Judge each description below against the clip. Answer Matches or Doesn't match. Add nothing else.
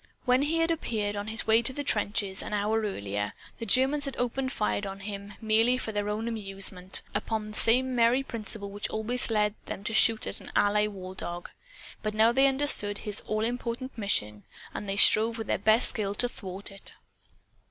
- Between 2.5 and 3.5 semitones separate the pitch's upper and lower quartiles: Matches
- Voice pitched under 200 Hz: Doesn't match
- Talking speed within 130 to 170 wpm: Doesn't match